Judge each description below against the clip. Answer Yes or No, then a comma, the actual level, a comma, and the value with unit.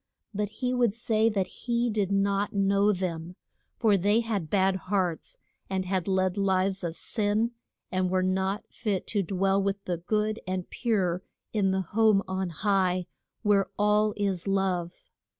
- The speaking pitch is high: Yes, high, 195 Hz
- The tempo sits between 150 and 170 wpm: Yes, average, 160 wpm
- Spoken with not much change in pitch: Yes, narrow, 2.0 semitones